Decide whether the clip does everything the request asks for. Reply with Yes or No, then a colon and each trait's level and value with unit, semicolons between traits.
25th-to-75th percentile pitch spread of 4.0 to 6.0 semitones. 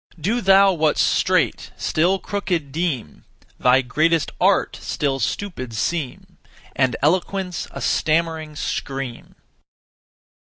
Yes: average, 5.1 semitones